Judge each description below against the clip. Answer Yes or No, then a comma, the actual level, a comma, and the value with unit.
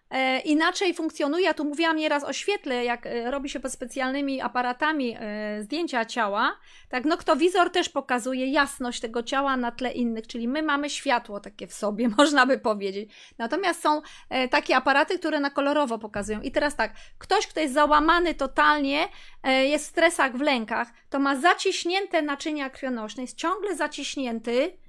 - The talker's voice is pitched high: Yes, very high, 280 Hz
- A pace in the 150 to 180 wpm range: Yes, fast, 160 wpm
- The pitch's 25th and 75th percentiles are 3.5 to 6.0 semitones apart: Yes, average, 4.0 semitones